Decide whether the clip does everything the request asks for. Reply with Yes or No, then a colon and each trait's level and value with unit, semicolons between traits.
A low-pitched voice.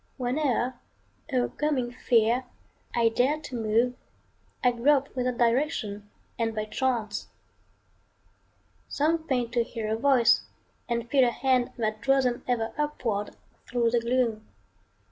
No: high, 245 Hz